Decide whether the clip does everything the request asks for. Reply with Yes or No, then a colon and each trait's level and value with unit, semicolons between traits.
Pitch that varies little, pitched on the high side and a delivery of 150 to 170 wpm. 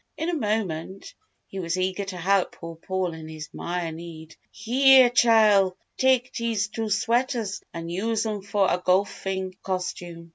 No: average, 4.2 semitones; high, 195 Hz; average, 155 wpm